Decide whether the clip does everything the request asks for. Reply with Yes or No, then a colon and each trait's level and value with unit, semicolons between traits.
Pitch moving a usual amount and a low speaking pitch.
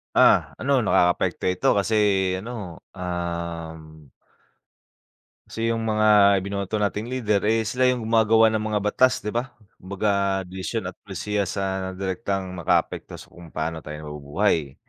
Yes: average, 3.8 semitones; low, 100 Hz